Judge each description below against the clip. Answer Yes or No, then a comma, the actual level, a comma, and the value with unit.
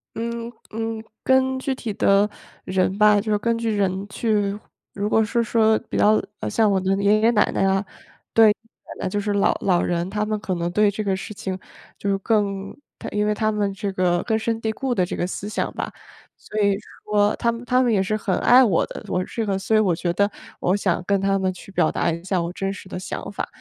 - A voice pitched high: Yes, high, 205 Hz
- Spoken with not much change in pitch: Yes, narrow, 2.3 semitones